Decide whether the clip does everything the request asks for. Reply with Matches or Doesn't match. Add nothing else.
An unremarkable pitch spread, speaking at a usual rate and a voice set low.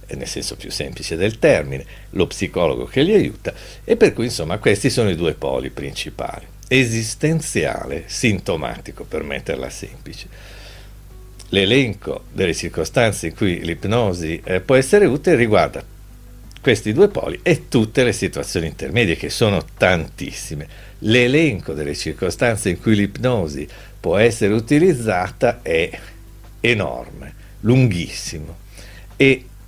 Matches